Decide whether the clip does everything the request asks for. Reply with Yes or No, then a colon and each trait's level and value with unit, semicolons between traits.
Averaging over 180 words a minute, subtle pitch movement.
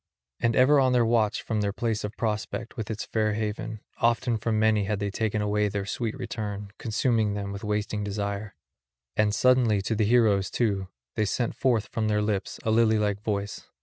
Yes: average, 195 wpm; narrow, 1.8 semitones